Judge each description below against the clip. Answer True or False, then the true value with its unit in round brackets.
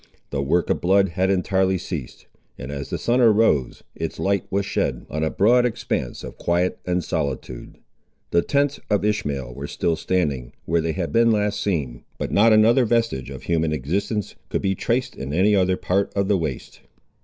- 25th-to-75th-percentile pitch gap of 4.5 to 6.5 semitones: True (5.2 semitones)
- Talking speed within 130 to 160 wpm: False (190 wpm)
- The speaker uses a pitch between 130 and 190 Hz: False (95 Hz)